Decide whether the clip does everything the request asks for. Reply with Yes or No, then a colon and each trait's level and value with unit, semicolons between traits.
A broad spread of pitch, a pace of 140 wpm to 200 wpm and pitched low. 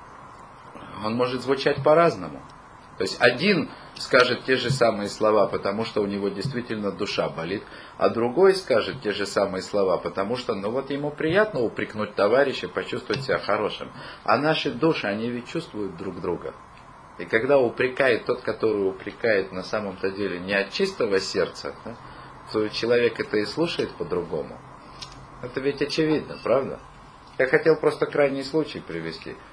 Yes: wide, 7.0 semitones; average, 150 wpm; low, 125 Hz